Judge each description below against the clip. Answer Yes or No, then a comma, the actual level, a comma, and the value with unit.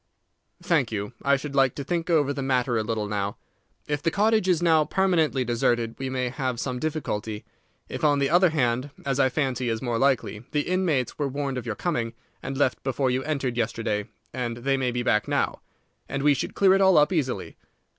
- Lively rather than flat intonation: No, average, 4.0 semitones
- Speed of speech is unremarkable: No, fast, 210 wpm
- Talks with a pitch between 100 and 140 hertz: Yes, low, 135 Hz